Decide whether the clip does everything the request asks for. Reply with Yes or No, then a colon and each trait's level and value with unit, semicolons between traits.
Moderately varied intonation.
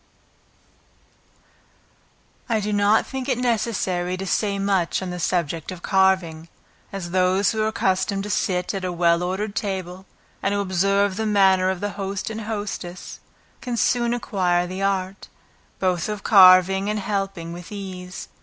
No: narrow, 2.1 semitones